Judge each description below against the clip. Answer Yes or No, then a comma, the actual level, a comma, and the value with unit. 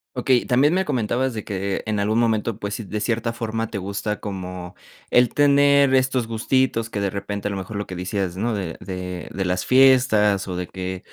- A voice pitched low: Yes, low, 105 Hz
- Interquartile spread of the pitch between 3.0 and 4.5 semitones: Yes, average, 4.1 semitones